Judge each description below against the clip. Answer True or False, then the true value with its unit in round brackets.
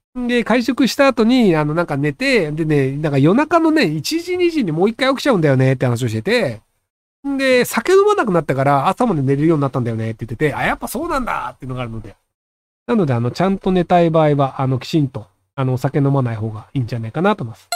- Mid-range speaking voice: True (150 Hz)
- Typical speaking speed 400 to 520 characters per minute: True (485 characters per minute)